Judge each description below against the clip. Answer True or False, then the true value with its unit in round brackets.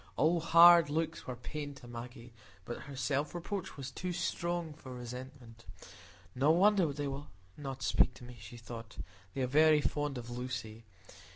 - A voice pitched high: False (135 Hz)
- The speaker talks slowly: False (170 wpm)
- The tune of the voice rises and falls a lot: False (4.3 semitones)